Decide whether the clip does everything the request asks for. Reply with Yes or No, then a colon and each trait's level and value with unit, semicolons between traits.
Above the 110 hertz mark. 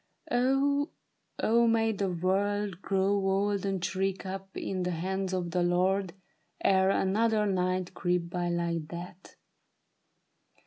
Yes: high, 190 Hz